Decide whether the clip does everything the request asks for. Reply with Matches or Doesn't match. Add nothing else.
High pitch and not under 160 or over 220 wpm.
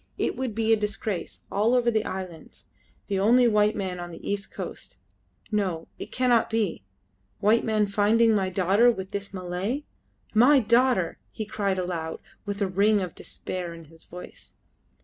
Matches